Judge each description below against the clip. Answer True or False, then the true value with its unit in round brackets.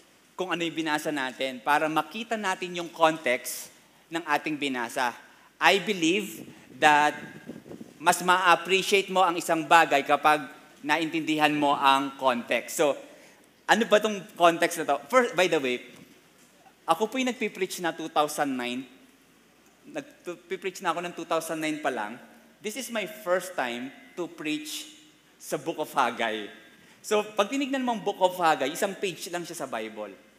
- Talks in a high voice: False (165 Hz)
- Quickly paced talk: False (150 wpm)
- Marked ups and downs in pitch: False (4.4 semitones)